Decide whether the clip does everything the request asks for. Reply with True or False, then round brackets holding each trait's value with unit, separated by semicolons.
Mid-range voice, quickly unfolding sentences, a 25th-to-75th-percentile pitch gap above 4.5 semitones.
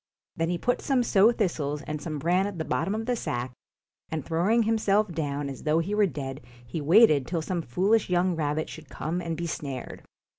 True (165 Hz; 210 wpm; 5.2 semitones)